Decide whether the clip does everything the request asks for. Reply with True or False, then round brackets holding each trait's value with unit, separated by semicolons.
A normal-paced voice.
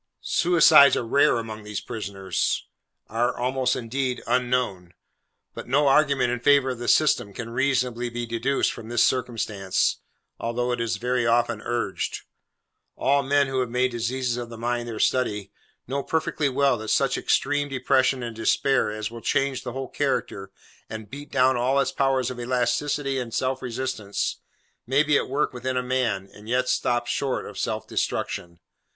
True (170 wpm)